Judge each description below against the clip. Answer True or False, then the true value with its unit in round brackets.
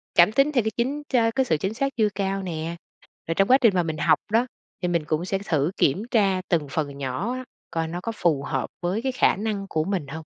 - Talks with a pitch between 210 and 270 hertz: False (190 Hz)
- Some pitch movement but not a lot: False (6.0 semitones)